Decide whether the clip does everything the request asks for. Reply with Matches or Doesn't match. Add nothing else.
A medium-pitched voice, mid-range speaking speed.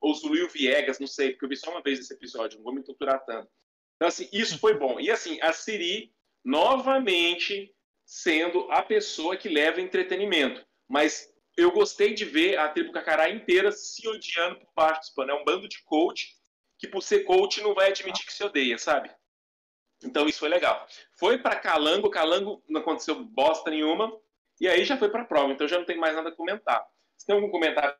Doesn't match